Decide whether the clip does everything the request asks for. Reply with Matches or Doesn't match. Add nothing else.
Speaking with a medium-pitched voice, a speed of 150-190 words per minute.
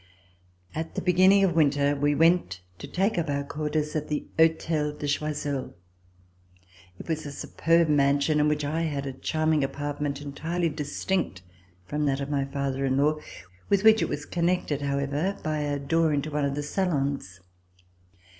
Matches